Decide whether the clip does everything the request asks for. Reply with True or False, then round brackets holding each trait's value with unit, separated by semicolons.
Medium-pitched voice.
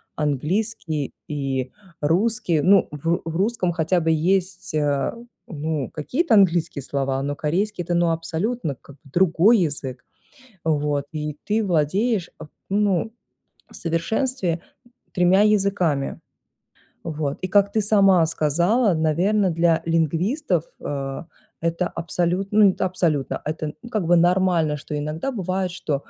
True (170 Hz)